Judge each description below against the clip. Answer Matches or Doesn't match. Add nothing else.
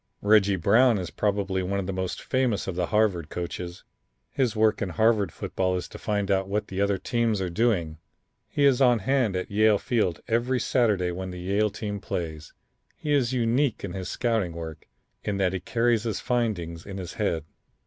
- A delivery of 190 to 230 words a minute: Matches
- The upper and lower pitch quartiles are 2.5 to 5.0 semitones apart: Matches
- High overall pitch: Doesn't match